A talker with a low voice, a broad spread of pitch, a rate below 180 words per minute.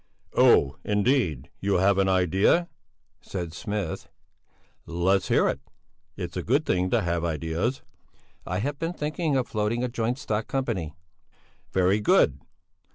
Yes: low, 100 Hz; wide, 5.9 semitones; average, 140 wpm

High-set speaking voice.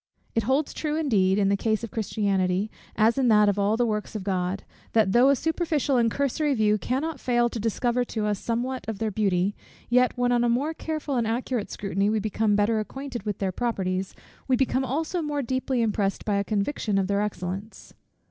Yes: high, 225 Hz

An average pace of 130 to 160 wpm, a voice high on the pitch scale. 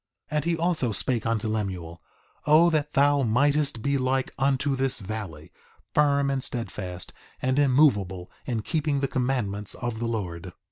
No: average, 155 wpm; low, 130 Hz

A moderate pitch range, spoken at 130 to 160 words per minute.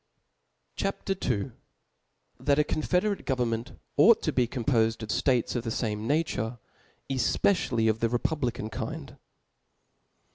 Yes: average, 4.6 semitones; average, 140 wpm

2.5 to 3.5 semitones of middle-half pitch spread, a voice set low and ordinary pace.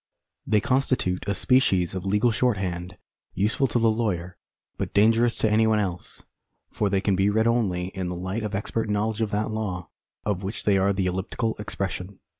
Yes: average, 3.0 semitones; low, 105 Hz; average, 190 wpm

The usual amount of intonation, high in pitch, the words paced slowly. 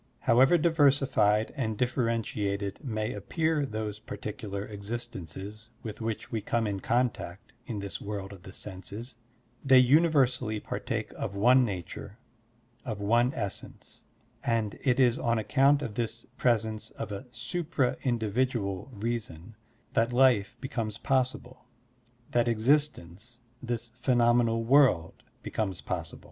No: average, 3.6 semitones; low, 115 Hz; slow, 130 wpm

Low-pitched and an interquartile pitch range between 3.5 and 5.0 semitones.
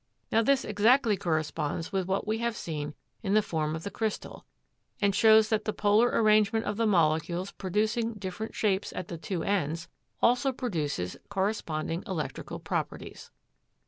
No: high, 200 Hz; average, 4.7 semitones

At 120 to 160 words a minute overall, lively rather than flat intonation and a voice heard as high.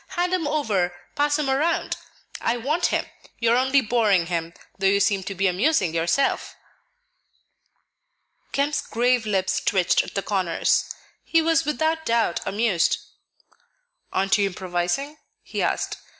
Yes: average, 140 wpm; wide, 7.5 semitones; high, 230 Hz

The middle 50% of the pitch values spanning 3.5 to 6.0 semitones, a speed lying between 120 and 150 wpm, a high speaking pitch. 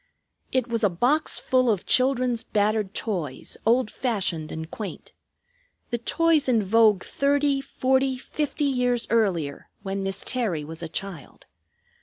Yes: average, 5.0 semitones; average, 140 wpm; high, 230 Hz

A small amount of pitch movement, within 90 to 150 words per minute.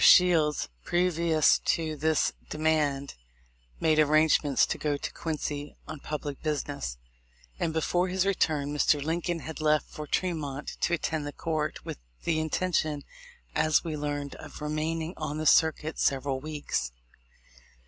Yes: narrow, 1.7 semitones; average, 140 wpm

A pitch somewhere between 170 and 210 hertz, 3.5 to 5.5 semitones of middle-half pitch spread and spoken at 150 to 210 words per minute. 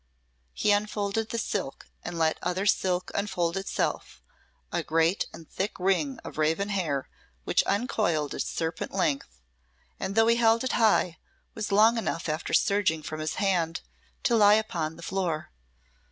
Yes: high, 190 Hz; average, 4.5 semitones; average, 155 wpm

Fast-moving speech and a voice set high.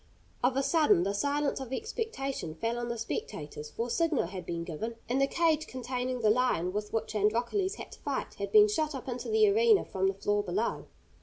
Yes: fast, 215 wpm; high, 245 Hz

